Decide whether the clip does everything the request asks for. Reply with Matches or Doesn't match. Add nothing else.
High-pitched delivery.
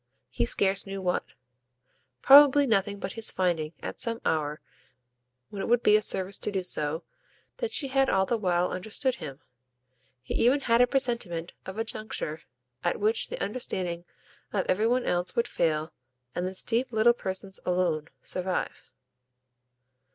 Matches